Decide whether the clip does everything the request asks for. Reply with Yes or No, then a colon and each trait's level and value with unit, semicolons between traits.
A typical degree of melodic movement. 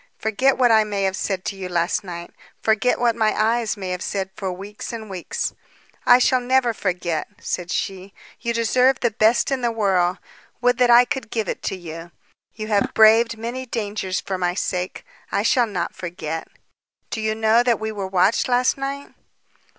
Yes: average, 4.1 semitones